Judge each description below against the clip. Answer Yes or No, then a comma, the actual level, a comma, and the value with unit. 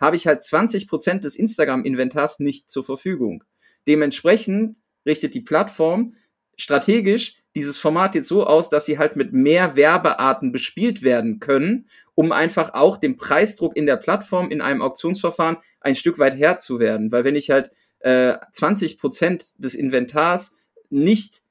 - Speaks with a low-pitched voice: No, medium, 160 Hz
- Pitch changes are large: Yes, wide, 6.7 semitones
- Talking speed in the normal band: Yes, average, 145 wpm